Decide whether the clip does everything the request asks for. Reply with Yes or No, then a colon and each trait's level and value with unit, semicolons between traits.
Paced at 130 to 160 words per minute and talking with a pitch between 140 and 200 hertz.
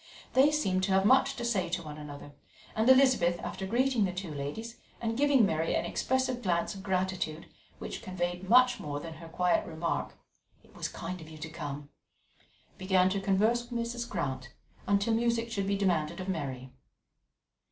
No: average, 180 wpm; high, 190 Hz